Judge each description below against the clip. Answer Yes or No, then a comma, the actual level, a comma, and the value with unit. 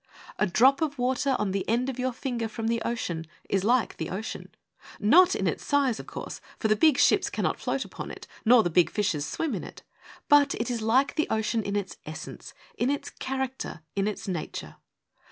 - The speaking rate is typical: No, fast, 210 wpm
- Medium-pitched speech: No, high, 230 Hz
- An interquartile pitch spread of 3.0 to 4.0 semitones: No, average, 4.4 semitones